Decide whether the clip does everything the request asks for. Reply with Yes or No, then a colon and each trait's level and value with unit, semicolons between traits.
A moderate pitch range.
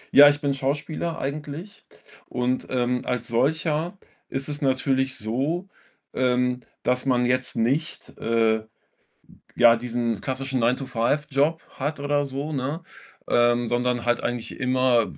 Yes: average, 3.0 semitones